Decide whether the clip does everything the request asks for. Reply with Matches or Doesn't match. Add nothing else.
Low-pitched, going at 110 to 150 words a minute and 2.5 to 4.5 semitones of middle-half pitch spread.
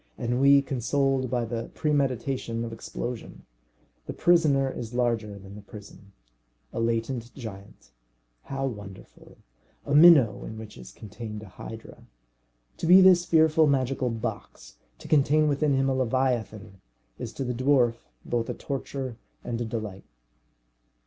Matches